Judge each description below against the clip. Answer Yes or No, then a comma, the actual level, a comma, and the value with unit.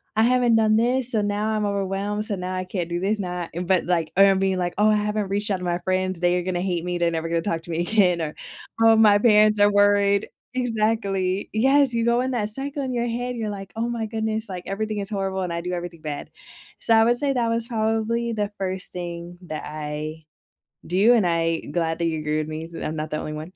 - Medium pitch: No, high, 200 Hz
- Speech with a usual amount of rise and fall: Yes, average, 4.1 semitones